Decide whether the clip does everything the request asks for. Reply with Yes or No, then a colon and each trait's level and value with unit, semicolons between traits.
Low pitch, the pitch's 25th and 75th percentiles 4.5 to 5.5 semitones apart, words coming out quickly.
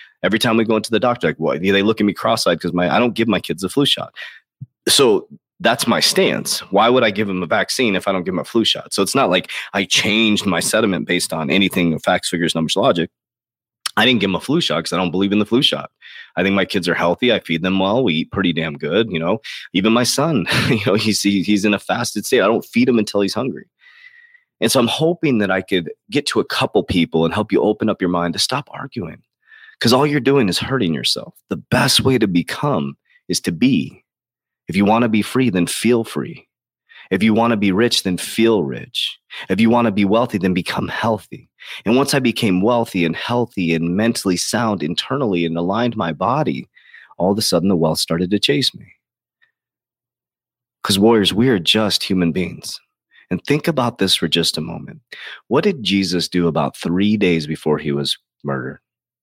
Yes: low, 100 Hz; average, 5.1 semitones; fast, 220 wpm